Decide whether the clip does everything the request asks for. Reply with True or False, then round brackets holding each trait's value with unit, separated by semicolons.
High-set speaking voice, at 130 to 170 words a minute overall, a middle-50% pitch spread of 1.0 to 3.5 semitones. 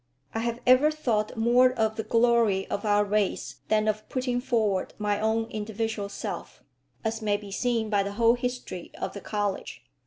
False (220 Hz; 180 wpm; 2.4 semitones)